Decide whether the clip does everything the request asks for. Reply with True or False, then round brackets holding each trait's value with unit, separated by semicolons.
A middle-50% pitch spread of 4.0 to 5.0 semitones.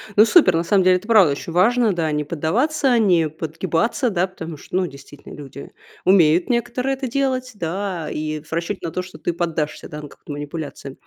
False (5.5 semitones)